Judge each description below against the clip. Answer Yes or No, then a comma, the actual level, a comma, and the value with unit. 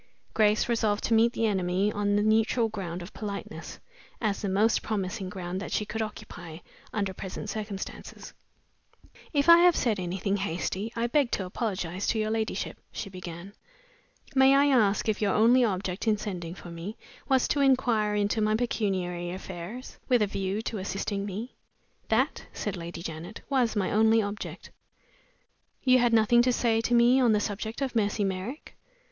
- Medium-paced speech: Yes, average, 175 wpm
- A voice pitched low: No, high, 210 Hz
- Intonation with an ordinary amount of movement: Yes, average, 3.3 semitones